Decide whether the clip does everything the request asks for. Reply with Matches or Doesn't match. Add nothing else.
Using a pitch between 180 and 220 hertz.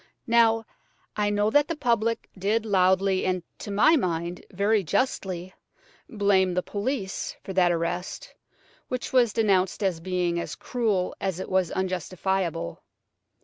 Matches